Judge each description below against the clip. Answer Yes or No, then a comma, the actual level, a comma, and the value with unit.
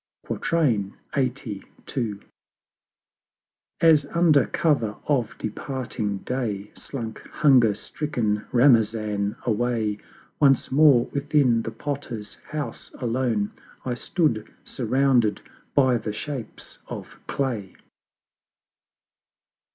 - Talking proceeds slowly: Yes, slow, 80 wpm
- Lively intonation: No, average, 4.5 semitones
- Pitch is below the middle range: Yes, low, 120 Hz